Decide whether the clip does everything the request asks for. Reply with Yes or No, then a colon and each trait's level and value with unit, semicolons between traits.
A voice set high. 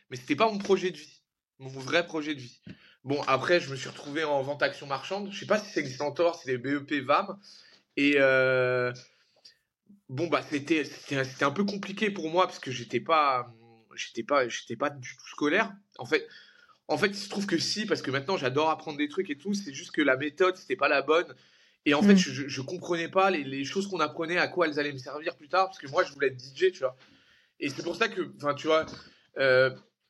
No: medium, 155 Hz